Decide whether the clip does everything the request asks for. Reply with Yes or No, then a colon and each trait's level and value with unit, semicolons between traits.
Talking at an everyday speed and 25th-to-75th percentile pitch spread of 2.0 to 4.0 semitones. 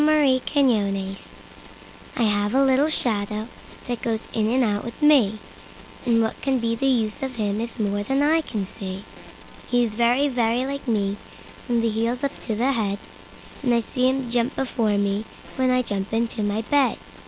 Yes: average, 175 wpm; average, 3.6 semitones